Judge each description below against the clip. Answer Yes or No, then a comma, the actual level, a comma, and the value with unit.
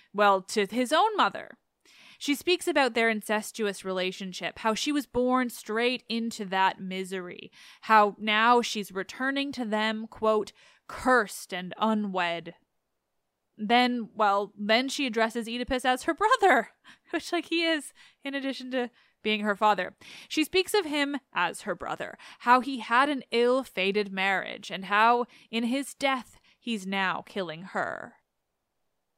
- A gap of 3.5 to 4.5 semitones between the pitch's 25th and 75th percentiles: Yes, average, 4.2 semitones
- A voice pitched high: Yes, high, 230 Hz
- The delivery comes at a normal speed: Yes, average, 145 wpm